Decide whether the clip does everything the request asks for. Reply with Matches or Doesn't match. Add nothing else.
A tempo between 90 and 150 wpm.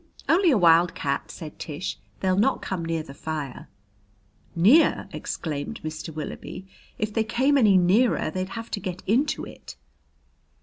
Matches